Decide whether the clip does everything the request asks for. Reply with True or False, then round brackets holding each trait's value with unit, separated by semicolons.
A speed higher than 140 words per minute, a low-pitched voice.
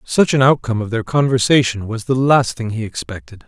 True (205 wpm; 120 Hz)